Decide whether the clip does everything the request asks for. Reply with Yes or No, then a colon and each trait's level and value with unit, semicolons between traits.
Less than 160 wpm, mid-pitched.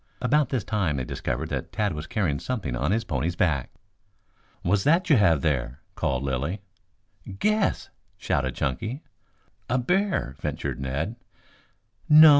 No: average, 140 wpm; very low, 95 Hz